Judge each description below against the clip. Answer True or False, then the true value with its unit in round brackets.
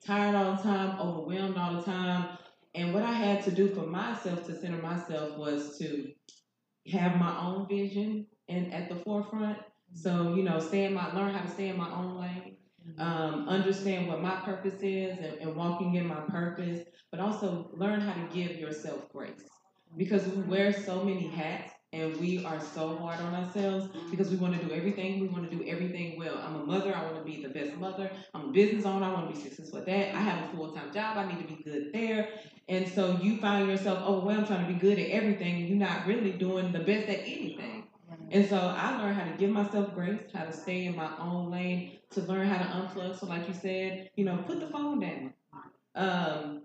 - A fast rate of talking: True (225 wpm)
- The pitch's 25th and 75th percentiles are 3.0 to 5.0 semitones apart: False (2.5 semitones)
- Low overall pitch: False (185 Hz)